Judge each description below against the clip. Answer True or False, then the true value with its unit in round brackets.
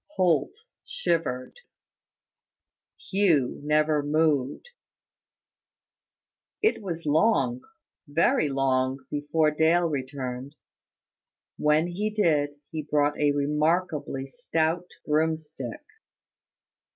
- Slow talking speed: True (80 wpm)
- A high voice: False (150 Hz)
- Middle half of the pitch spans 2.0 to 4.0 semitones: True (2.7 semitones)